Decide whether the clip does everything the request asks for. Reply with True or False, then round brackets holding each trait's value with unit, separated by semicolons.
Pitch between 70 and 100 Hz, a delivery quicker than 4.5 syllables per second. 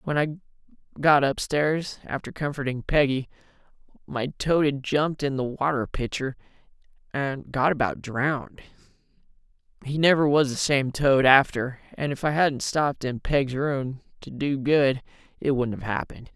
False (140 Hz; 4.7 syllables/s)